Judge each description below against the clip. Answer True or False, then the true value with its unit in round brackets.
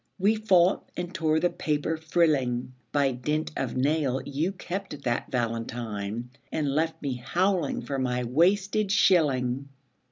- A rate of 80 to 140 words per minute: True (135 wpm)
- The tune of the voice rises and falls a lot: True (5.7 semitones)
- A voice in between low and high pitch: True (150 Hz)